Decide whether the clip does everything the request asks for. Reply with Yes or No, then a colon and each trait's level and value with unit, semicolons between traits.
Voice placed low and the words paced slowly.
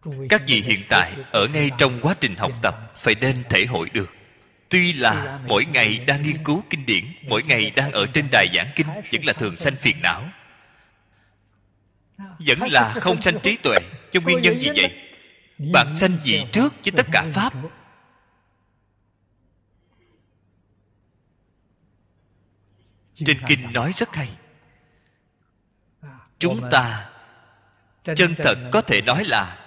Yes: low, 120 Hz; slow, 145 wpm